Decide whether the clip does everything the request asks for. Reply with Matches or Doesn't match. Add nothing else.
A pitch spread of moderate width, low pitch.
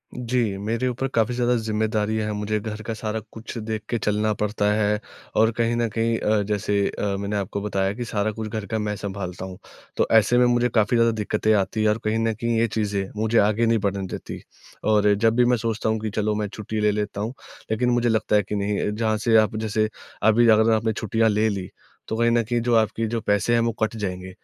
Doesn't match